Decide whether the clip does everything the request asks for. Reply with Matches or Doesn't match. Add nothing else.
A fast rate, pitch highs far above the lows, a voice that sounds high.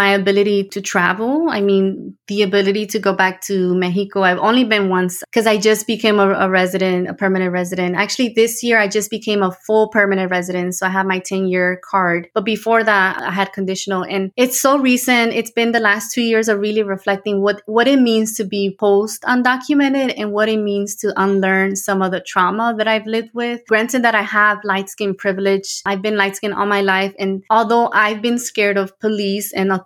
Doesn't match